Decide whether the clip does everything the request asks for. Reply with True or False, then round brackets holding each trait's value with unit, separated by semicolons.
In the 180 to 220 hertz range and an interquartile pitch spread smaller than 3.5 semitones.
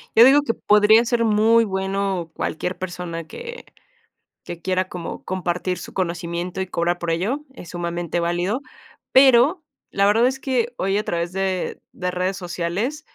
False (190 Hz; 4.7 semitones)